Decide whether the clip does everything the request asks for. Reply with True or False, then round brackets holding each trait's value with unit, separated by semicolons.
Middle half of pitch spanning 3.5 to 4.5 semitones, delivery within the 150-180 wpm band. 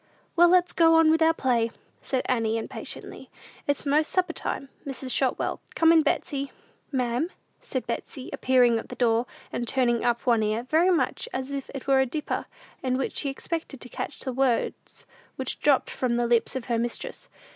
False (4.0 semitones; 190 wpm)